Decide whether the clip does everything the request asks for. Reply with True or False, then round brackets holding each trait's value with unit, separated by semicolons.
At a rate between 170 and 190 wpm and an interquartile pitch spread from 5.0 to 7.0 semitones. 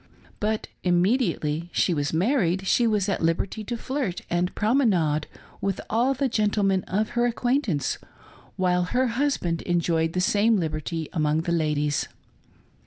False (145 wpm; 5.5 semitones)